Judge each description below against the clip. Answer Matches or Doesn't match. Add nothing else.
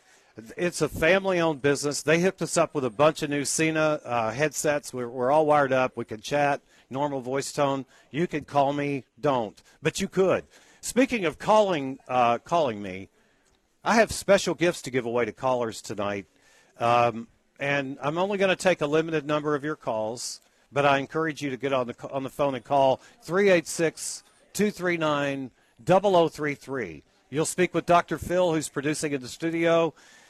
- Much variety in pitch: Doesn't match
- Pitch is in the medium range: Matches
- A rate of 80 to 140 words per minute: Doesn't match